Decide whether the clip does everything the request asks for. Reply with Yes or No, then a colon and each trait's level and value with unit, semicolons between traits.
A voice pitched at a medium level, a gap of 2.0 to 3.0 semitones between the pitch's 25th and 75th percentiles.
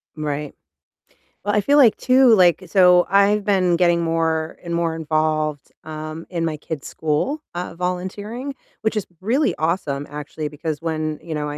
No: medium, 170 Hz; average, 4.2 semitones